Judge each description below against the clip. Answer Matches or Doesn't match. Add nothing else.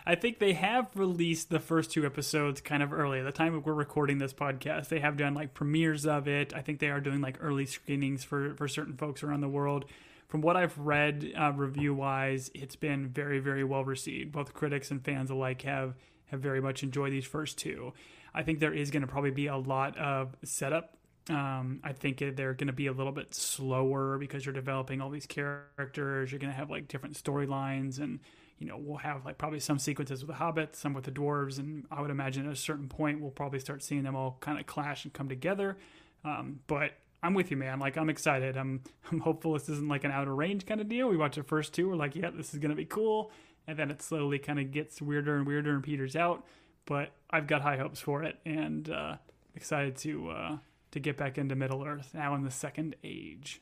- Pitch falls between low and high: Matches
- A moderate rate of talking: Doesn't match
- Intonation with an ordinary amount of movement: Doesn't match